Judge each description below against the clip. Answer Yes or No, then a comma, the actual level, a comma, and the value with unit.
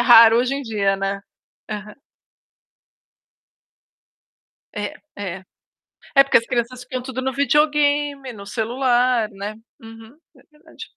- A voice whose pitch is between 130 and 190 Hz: No, high, 240 Hz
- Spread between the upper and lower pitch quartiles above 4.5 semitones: No, average, 4.2 semitones